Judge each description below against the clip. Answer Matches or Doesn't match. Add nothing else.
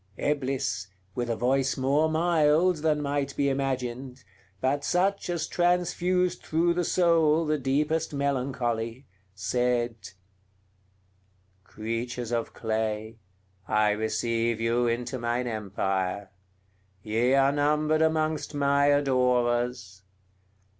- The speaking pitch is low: Matches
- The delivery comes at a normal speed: Doesn't match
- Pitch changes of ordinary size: Matches